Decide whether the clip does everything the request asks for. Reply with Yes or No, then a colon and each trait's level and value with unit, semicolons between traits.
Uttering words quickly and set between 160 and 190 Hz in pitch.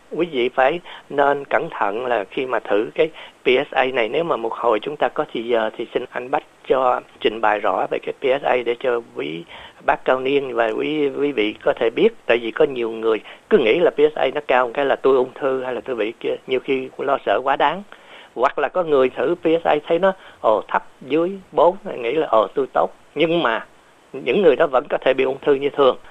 No: average, 235 wpm; medium, 185 Hz